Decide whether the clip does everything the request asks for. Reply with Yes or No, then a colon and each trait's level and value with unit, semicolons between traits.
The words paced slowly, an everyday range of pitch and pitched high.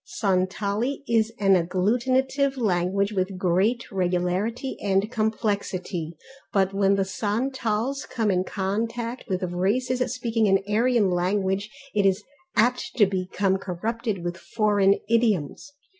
Yes: slow, 120 wpm; average, 3.6 semitones; high, 205 Hz